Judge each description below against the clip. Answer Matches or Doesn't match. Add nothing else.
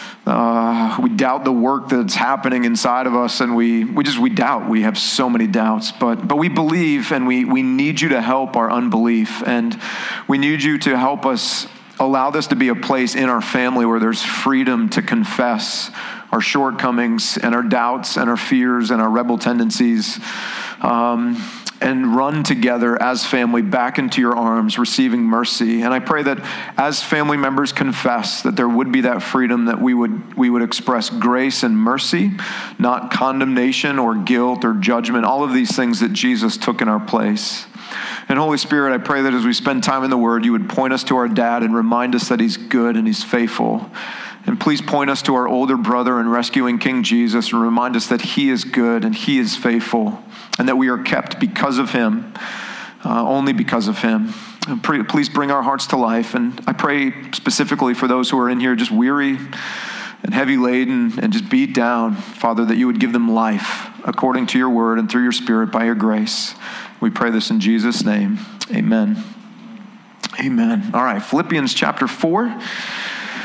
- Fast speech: Doesn't match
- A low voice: Doesn't match